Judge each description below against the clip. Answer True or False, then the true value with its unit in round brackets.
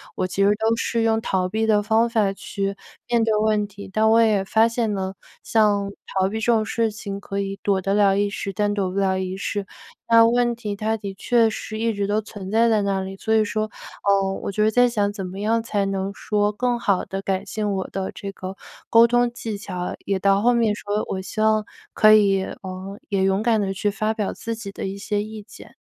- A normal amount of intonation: False (2.1 semitones)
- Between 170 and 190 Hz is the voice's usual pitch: False (205 Hz)